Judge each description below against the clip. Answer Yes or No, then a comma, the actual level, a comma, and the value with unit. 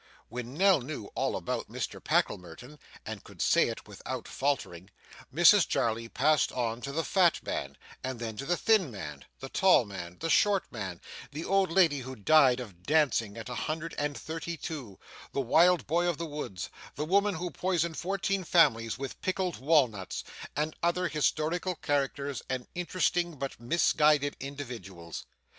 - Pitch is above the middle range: No, medium, 145 Hz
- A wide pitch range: Yes, wide, 6.1 semitones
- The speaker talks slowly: No, average, 165 wpm